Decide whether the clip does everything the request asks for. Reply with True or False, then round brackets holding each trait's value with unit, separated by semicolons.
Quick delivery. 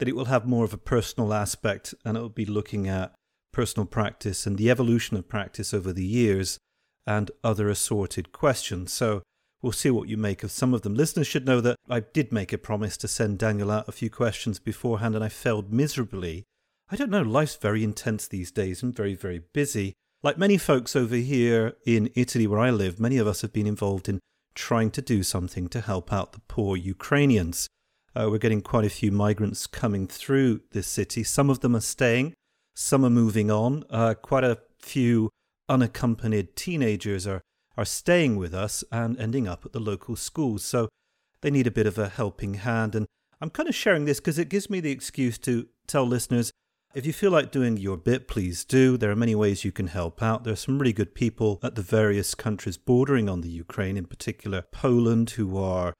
True (210 wpm)